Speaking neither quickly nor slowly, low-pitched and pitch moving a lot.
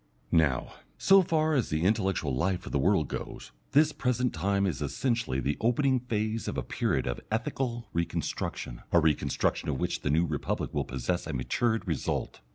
Yes: average, 175 wpm; very low, 95 Hz; wide, 7.9 semitones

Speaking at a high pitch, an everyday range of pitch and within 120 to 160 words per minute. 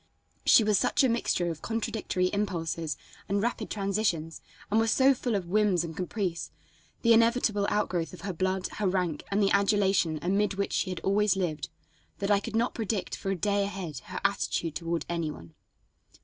No: high, 195 Hz; average, 3.4 semitones; average, 185 wpm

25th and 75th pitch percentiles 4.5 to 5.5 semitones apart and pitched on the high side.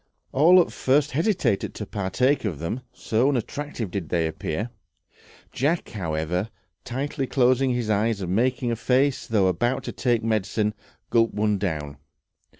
No: average, 5.1 semitones; low, 115 Hz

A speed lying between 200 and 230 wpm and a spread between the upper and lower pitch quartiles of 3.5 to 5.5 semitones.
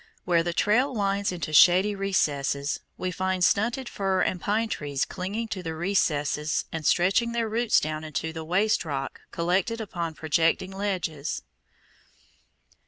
No: average, 145 wpm; average, 4.3 semitones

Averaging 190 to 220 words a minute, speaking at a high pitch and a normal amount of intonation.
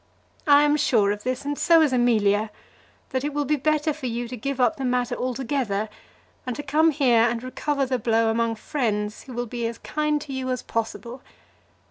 Yes: fast, 205 wpm; very high, 255 Hz; average, 4.0 semitones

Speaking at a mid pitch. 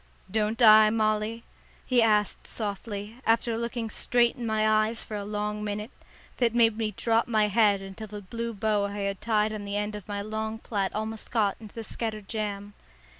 No: high, 215 Hz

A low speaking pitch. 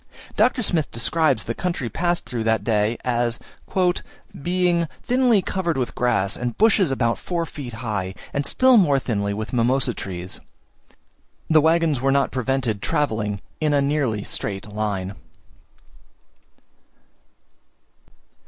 Yes: low, 125 Hz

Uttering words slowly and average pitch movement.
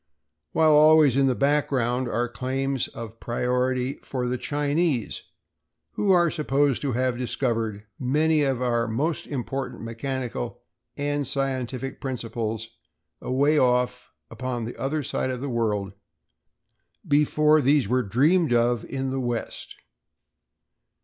Yes: slow, 125 wpm; average, 3.1 semitones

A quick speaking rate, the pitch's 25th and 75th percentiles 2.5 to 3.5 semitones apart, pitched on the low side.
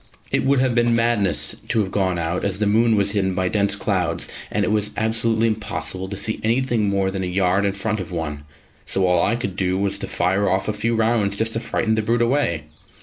Yes: fast, 235 wpm; average, 3.0 semitones; low, 100 Hz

